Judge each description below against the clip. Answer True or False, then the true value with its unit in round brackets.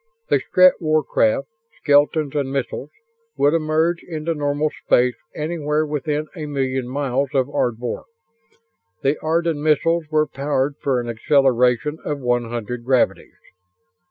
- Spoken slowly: True (130 wpm)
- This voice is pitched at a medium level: True (145 Hz)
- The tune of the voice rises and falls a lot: False (3.1 semitones)